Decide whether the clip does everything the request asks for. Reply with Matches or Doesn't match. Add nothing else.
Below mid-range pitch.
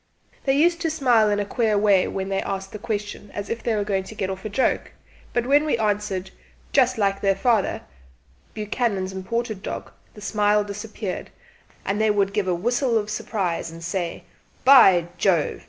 Doesn't match